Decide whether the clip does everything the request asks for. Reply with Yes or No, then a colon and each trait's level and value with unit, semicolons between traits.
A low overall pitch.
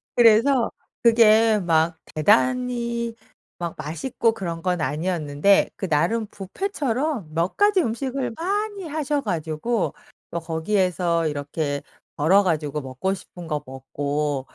No: medium, 185 Hz